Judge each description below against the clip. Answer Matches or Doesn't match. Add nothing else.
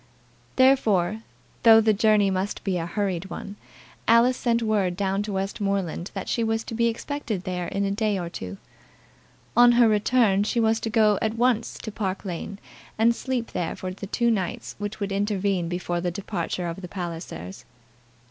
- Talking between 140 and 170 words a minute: Doesn't match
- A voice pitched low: Doesn't match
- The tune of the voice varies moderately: Matches